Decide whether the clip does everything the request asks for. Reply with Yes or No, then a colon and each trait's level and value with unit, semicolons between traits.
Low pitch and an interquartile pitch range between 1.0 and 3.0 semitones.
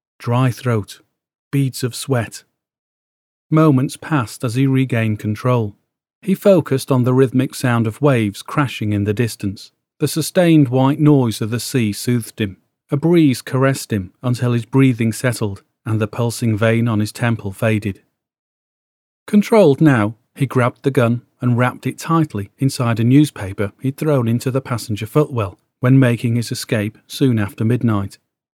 No: low, 125 Hz; average, 3.8 semitones